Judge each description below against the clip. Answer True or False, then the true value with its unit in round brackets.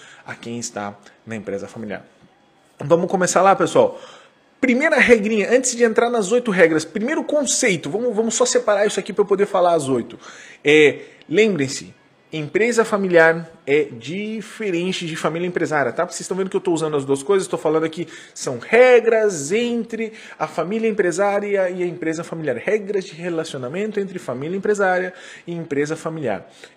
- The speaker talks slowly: False (165 wpm)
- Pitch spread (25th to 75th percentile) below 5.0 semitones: False (5.5 semitones)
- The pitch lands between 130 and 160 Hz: False (190 Hz)